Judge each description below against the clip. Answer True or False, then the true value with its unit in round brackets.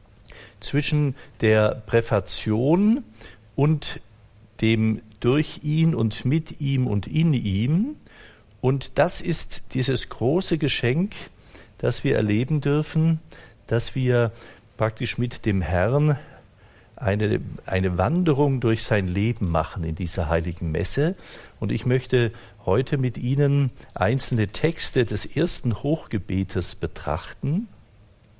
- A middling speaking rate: False (110 wpm)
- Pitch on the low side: True (120 Hz)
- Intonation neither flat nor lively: False (6.0 semitones)